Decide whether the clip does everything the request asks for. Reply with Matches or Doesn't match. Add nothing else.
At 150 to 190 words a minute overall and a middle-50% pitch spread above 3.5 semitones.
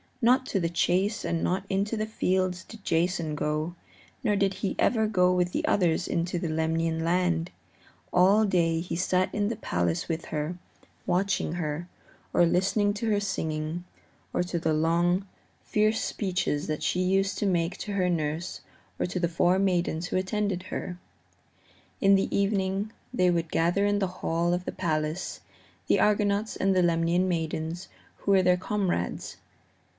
Doesn't match